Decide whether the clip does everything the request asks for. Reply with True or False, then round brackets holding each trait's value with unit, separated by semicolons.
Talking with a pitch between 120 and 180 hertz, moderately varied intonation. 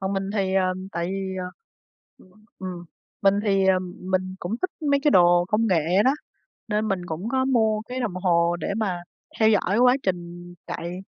False (190 Hz; 3.3 semitones)